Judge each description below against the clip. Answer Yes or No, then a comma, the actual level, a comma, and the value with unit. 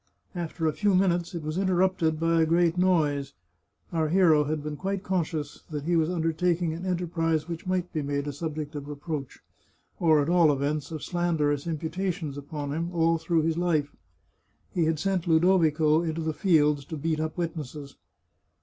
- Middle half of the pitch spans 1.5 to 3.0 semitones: Yes, narrow, 2.5 semitones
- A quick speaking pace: No, average, 175 wpm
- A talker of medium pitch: Yes, medium, 160 Hz